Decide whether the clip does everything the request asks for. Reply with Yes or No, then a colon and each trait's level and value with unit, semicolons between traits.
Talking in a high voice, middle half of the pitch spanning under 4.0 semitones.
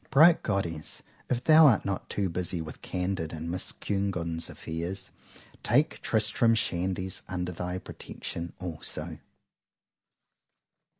No: very low, 90 Hz; average, 3.3 semitones